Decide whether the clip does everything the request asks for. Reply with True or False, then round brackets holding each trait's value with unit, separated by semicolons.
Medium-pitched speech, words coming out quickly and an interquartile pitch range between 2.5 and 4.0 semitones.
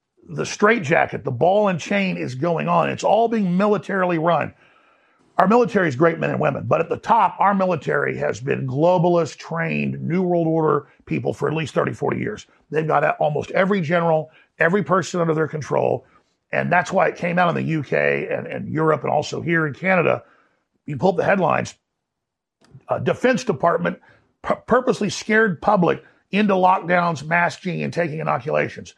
False (175 Hz; 175 wpm; 3.3 semitones)